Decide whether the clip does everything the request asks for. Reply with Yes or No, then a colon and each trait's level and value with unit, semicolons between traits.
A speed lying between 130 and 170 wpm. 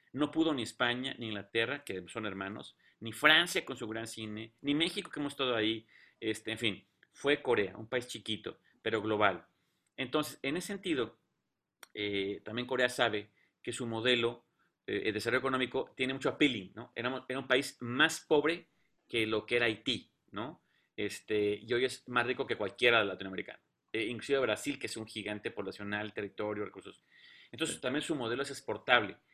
No: average, 180 wpm